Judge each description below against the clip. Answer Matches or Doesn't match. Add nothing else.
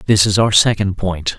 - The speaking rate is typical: Doesn't match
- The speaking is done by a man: Matches